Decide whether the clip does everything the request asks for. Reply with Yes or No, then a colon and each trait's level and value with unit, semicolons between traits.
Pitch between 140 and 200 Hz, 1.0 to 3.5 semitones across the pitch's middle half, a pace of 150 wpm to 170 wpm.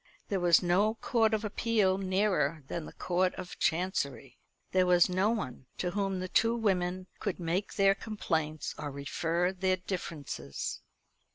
Yes: medium, 185 Hz; average, 3.0 semitones; average, 155 wpm